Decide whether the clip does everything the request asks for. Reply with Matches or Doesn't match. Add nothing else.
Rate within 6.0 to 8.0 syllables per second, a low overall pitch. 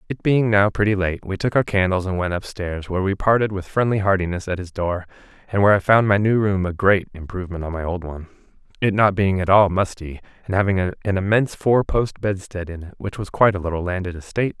Matches